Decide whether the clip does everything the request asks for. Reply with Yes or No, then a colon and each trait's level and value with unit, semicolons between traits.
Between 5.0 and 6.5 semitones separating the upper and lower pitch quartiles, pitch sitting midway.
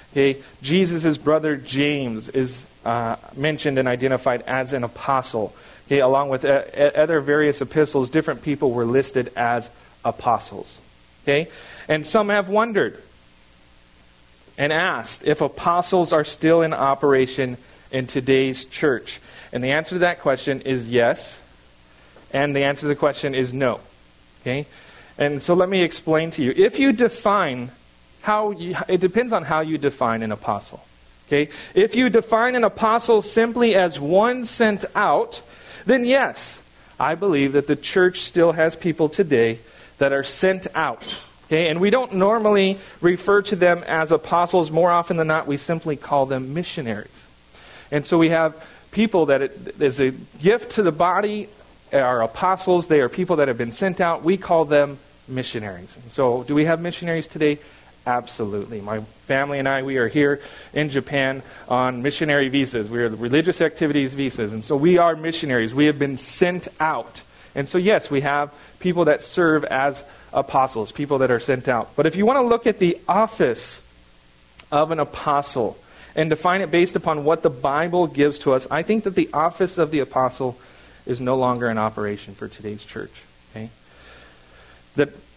Yes: wide, 5.6 semitones; medium, 145 Hz